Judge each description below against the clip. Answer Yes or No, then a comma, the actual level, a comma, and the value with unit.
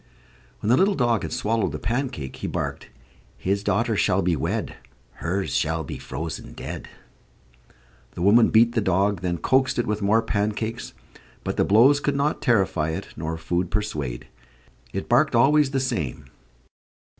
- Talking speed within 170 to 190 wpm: No, average, 160 wpm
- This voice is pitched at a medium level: No, low, 105 Hz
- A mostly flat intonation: No, wide, 5.5 semitones